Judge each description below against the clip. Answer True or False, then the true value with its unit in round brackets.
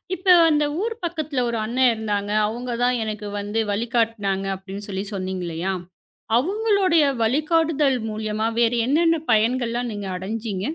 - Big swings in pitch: True (6.3 semitones)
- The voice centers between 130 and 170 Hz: False (230 Hz)